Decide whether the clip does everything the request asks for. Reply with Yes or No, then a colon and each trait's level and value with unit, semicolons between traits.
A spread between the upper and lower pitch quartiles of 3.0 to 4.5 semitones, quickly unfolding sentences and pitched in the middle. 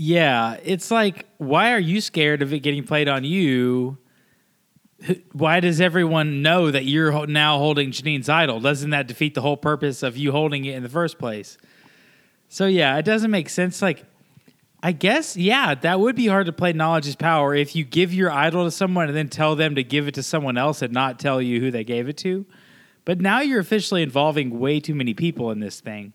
Yes: average, 4.2 semitones; fast, 215 wpm; medium, 155 Hz